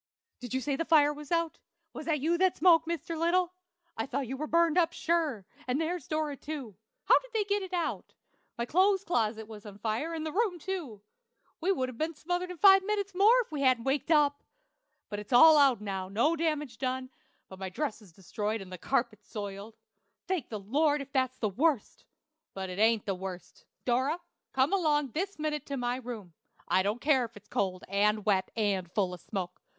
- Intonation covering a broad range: Yes, wide, 7.5 semitones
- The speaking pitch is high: Yes, very high, 270 Hz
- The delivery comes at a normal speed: No, fast, 210 wpm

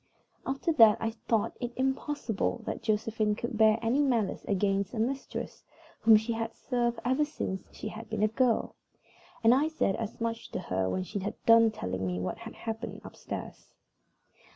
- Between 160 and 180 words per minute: Yes, average, 175 wpm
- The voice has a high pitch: Yes, high, 225 Hz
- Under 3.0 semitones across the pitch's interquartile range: Yes, narrow, 2.5 semitones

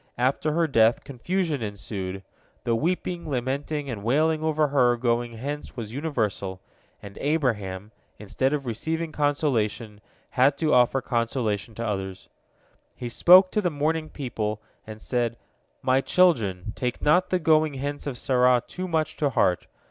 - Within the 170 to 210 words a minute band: No, average, 150 wpm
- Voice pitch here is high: No, low, 130 Hz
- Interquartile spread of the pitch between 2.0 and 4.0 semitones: No, average, 5.3 semitones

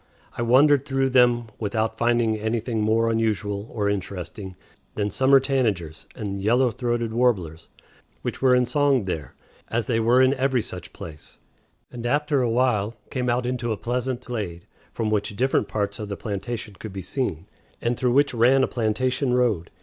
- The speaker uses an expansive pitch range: No, average, 3.5 semitones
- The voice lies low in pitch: Yes, low, 115 Hz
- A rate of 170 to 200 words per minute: Yes, average, 175 wpm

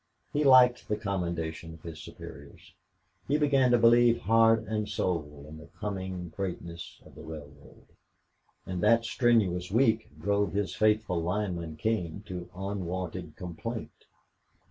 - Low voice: Yes, very low, 95 Hz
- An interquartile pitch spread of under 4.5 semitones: No, average, 4.9 semitones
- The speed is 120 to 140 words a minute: Yes, slow, 135 wpm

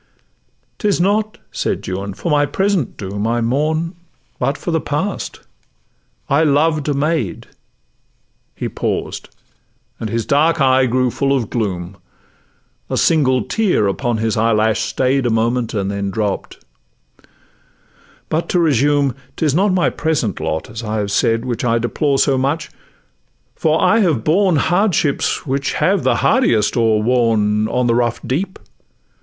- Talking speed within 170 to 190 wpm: No, average, 145 wpm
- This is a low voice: Yes, low, 130 Hz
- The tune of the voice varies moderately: No, wide, 5.9 semitones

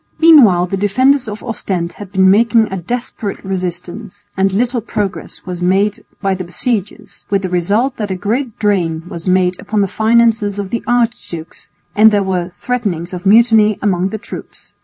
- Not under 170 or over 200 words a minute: Yes, average, 175 wpm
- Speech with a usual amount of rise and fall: Yes, average, 3.5 semitones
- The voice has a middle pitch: No, high, 200 Hz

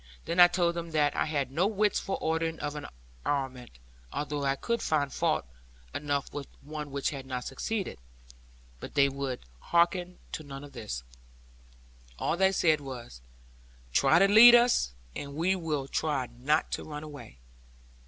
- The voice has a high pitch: No, medium, 150 Hz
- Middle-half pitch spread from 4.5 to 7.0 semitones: No, average, 3.9 semitones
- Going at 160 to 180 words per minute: Yes, average, 170 wpm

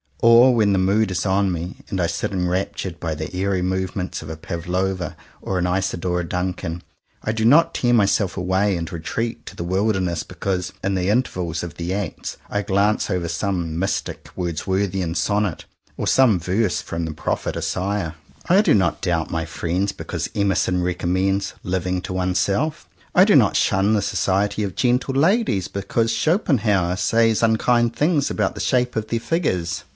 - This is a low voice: Yes, very low, 95 Hz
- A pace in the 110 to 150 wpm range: No, average, 175 wpm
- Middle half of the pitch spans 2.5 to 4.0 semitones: Yes, average, 3.4 semitones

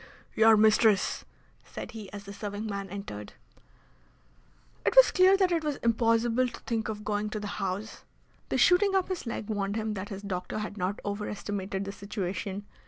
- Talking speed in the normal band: Yes, average, 175 wpm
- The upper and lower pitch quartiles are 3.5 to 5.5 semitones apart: No, narrow, 2.4 semitones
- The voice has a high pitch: Yes, high, 210 Hz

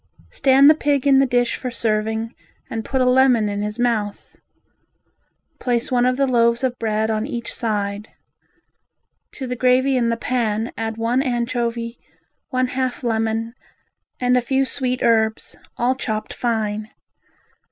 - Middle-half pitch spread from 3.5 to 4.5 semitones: No, narrow, 2.4 semitones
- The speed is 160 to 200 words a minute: No, average, 150 wpm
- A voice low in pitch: No, high, 240 Hz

